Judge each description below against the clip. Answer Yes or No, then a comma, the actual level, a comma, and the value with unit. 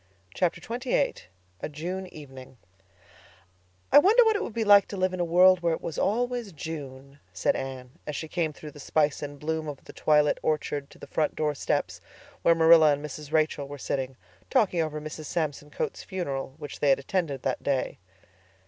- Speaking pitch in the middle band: Yes, medium, 155 Hz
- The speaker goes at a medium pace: Yes, average, 195 wpm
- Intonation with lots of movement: No, average, 4.0 semitones